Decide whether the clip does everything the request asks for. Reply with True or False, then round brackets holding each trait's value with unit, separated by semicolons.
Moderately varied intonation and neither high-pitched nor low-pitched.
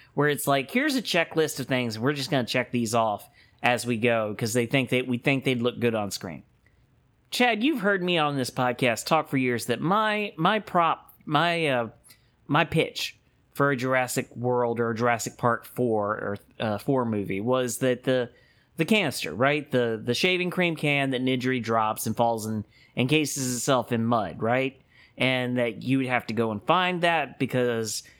False (3.6 semitones; 125 Hz)